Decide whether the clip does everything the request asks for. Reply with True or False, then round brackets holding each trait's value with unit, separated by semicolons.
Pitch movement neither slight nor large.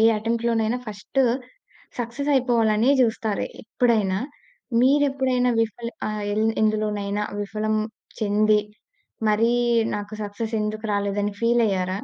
False (2.2 semitones)